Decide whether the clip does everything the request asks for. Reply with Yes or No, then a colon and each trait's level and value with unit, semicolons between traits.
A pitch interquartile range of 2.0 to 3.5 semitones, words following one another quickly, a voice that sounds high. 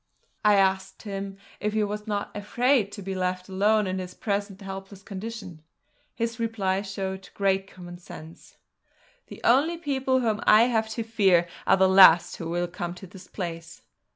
No: narrow, 2.6 semitones; average, 170 wpm; high, 195 Hz